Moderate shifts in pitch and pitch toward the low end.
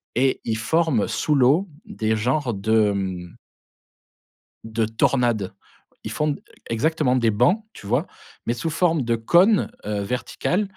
No: wide, 5.9 semitones; low, 120 Hz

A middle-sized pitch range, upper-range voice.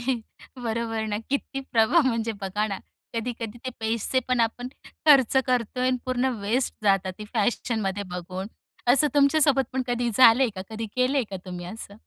Yes: average, 3.4 semitones; high, 230 Hz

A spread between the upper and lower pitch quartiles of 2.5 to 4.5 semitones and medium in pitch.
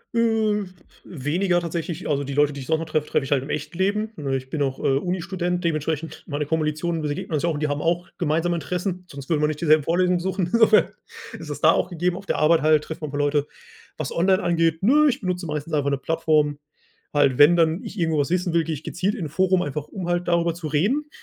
Yes: average, 3.3 semitones; medium, 165 Hz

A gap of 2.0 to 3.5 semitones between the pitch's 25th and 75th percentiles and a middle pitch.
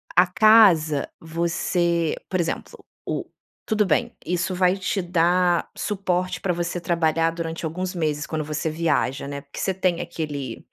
Yes: narrow, 2.5 semitones; medium, 170 Hz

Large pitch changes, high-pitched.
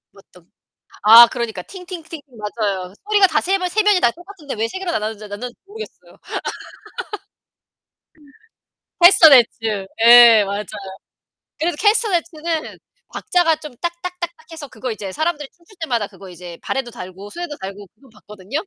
Yes: wide, 8.7 semitones; very high, 270 Hz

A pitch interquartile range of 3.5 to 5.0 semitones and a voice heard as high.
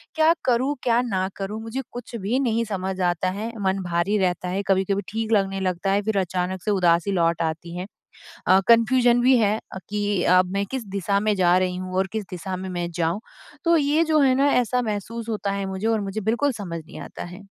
Yes: average, 3.8 semitones; high, 200 Hz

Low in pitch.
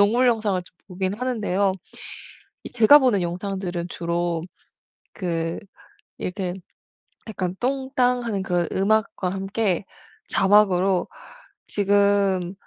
No: high, 195 Hz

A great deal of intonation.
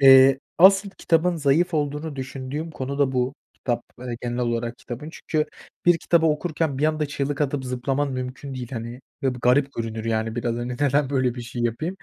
No: average, 3.4 semitones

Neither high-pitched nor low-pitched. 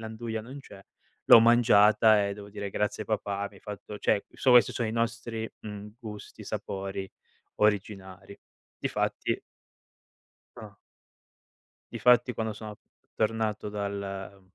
No: low, 105 Hz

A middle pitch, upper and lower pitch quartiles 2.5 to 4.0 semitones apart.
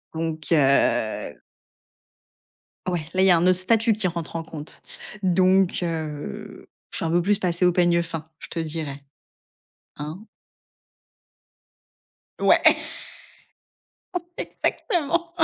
Yes: medium, 170 Hz; average, 2.8 semitones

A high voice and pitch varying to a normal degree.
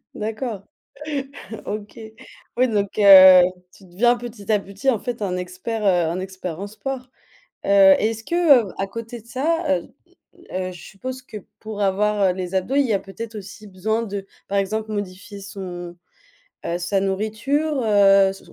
Yes: high, 205 Hz; average, 3.1 semitones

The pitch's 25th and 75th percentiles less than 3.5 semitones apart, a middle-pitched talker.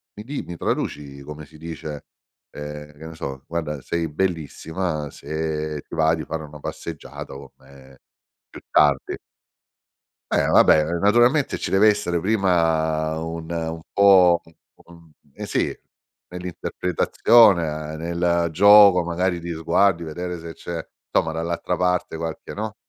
No: narrow, 2.5 semitones; very low, 85 Hz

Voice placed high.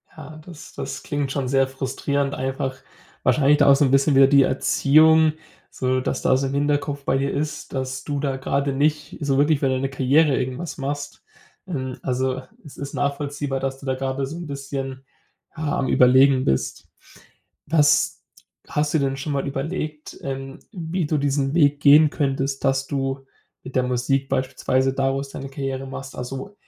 No: low, 135 Hz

